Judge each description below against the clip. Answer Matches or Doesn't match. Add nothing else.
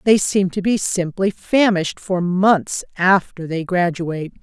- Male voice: Doesn't match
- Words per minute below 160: Matches